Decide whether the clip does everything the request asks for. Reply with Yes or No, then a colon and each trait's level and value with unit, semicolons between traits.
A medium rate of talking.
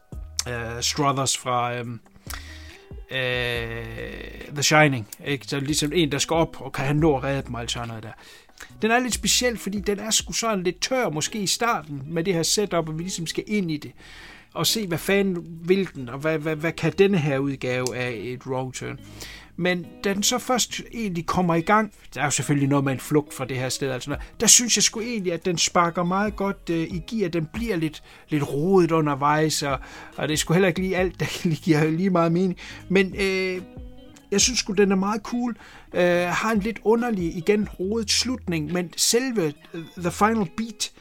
Yes: average, 205 wpm